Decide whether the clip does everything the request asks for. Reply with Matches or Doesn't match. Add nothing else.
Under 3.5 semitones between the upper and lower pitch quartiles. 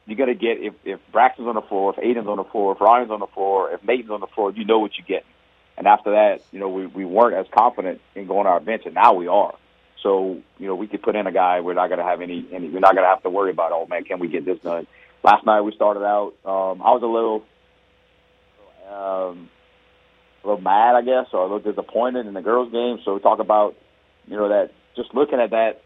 Matches